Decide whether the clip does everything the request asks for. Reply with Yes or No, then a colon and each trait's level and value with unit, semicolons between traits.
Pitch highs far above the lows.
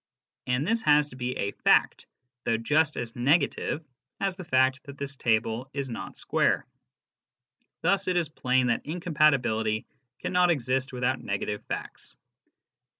No: average, 3.9 semitones